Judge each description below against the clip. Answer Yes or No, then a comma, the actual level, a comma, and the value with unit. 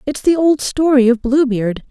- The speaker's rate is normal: Yes, average, 190 wpm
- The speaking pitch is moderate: No, very high, 265 Hz